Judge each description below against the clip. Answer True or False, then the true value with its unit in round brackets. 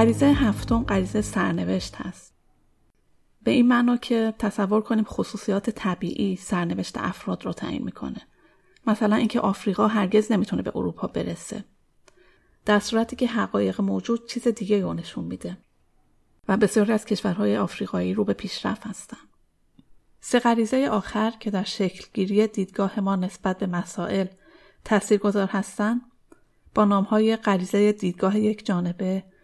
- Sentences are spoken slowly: False (130 wpm)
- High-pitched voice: True (205 Hz)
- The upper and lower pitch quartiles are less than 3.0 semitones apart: True (2.6 semitones)